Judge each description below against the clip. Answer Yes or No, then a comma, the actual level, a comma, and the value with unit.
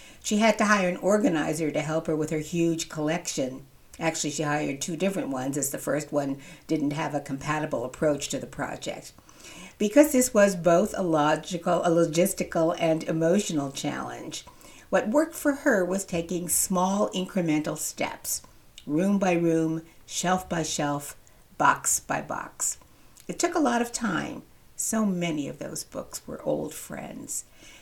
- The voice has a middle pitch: Yes, medium, 170 Hz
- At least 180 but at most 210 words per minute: No, average, 160 wpm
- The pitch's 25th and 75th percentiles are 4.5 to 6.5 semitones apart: No, average, 3.6 semitones